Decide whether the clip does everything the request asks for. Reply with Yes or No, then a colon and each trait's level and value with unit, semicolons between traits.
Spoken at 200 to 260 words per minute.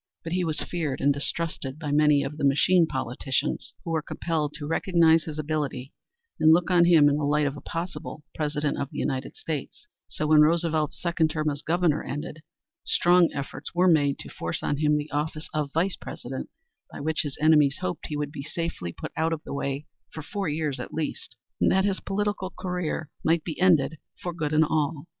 Yes: fast, 205 wpm